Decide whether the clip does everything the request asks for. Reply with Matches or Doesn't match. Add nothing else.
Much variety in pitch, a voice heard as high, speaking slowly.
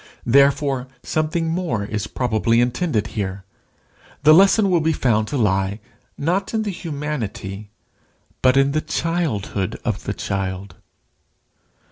Doesn't match